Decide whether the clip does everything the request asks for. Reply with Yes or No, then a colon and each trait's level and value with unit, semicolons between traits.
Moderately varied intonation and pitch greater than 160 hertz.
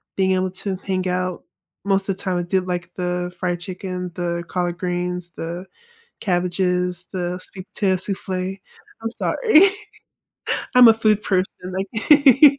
No: narrow, 1.5 semitones; medium, 185 Hz